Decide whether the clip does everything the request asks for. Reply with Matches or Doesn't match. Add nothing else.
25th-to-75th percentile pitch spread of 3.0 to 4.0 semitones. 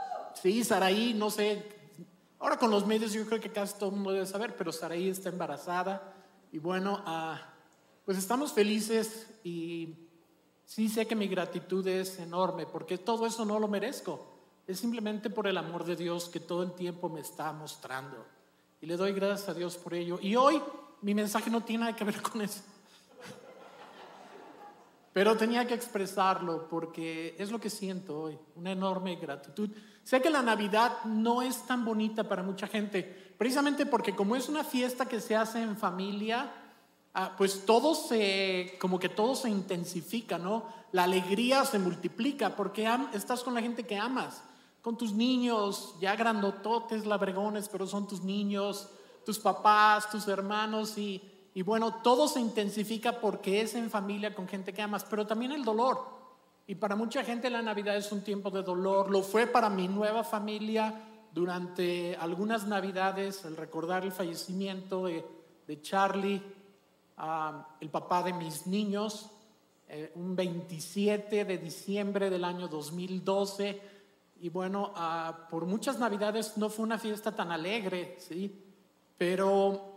Matches